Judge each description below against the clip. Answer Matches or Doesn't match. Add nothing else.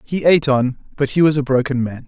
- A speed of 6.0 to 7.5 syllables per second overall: Matches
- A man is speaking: Matches